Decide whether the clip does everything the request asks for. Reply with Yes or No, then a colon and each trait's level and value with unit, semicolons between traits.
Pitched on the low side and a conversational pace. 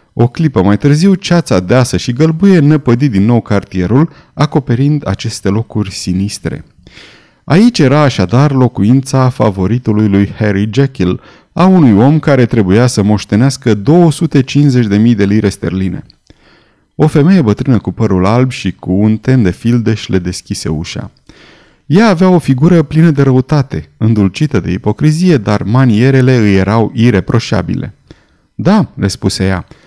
Yes: low, 120 Hz; average, 140 wpm